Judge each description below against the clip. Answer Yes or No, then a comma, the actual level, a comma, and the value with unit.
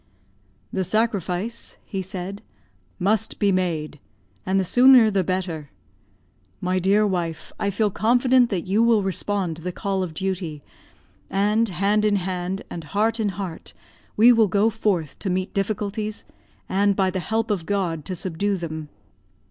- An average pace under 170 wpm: Yes, average, 155 wpm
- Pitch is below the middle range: No, high, 195 Hz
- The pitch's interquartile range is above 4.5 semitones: No, average, 2.8 semitones